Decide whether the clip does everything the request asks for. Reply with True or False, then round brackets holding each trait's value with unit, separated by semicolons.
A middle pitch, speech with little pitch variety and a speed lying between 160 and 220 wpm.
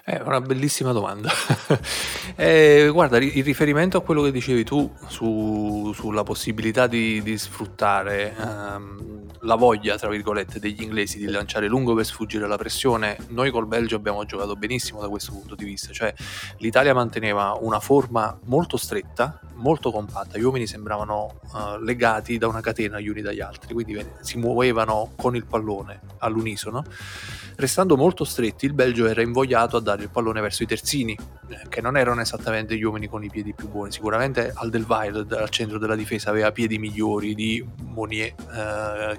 False (110 Hz; 2.2 semitones; 170 wpm)